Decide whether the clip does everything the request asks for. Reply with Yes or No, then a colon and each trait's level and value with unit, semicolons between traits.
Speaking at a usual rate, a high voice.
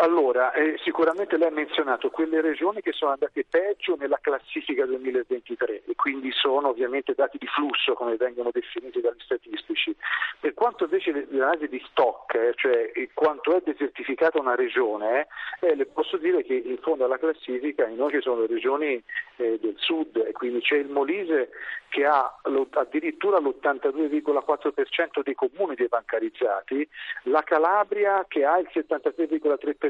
Yes: average, 140 wpm; very high, 325 Hz